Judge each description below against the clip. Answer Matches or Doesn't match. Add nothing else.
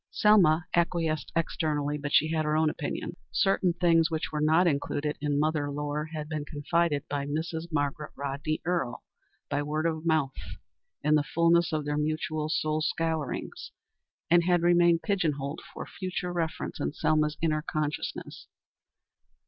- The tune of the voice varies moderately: Doesn't match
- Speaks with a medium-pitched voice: Matches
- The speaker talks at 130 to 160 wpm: Matches